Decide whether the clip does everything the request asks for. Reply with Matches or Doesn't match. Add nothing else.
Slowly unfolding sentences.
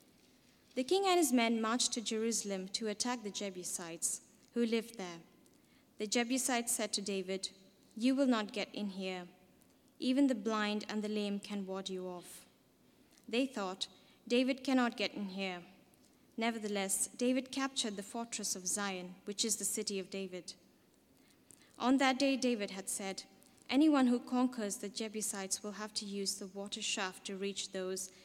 Doesn't match